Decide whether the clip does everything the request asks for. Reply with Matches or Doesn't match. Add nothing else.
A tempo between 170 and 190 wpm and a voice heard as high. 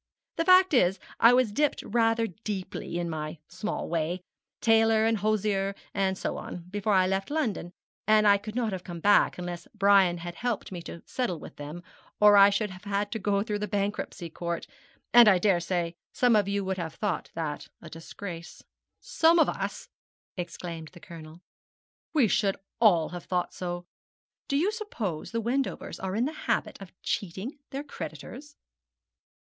Matches